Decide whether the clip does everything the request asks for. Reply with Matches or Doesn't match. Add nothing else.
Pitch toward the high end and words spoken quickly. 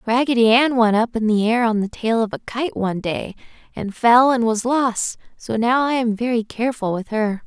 Matches